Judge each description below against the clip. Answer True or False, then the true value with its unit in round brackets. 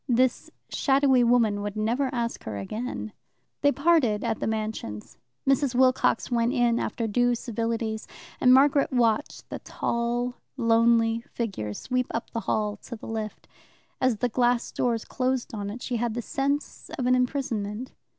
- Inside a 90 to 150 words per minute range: False (160 wpm)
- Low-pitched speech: False (235 Hz)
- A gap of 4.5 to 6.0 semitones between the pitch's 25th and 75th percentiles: False (2.5 semitones)